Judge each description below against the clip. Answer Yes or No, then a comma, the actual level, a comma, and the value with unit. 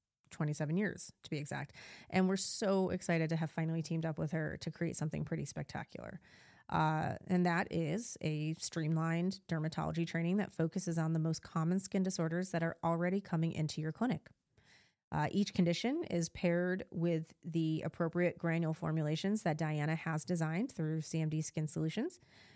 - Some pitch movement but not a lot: No, narrow, 2.1 semitones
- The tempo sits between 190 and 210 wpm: No, average, 165 wpm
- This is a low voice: No, medium, 165 Hz